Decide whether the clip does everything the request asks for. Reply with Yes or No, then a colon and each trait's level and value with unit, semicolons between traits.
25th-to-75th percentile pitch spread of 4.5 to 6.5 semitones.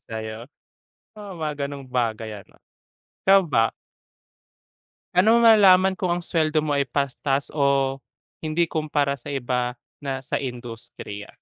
Yes: average, 4.8 semitones